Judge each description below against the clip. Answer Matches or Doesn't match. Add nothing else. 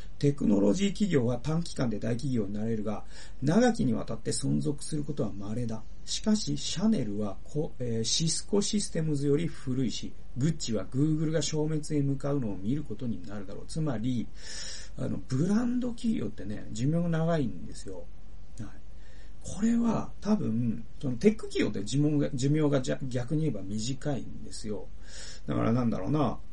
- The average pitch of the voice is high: Doesn't match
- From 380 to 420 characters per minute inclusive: Doesn't match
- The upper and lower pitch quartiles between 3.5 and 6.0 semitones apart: Doesn't match